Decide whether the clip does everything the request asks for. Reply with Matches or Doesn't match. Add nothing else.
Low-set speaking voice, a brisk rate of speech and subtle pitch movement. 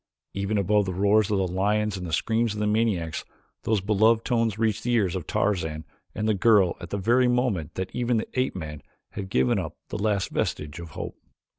Doesn't match